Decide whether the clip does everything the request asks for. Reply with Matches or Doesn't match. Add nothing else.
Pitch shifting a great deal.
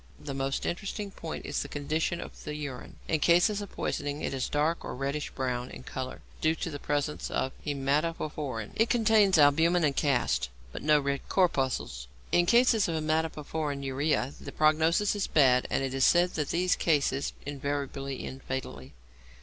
Doesn't match